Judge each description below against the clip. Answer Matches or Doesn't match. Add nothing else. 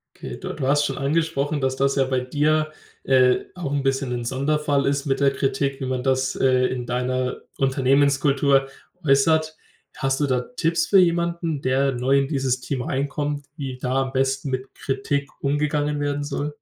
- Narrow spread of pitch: Matches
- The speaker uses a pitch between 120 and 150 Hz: Matches